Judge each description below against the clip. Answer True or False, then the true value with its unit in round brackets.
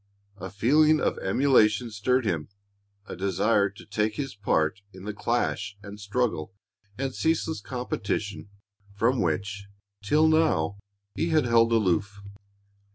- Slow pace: True (130 wpm)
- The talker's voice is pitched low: True (105 Hz)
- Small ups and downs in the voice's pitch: False (4.2 semitones)